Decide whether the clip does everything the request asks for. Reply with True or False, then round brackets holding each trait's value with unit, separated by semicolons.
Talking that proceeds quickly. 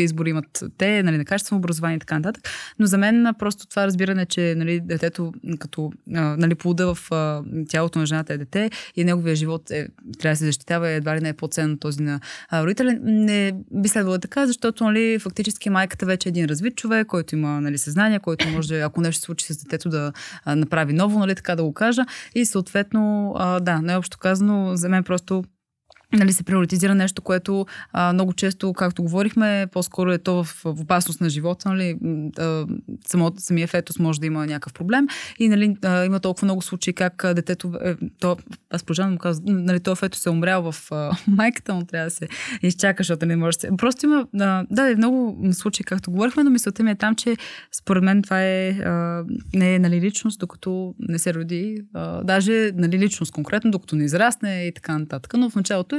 True (205 wpm)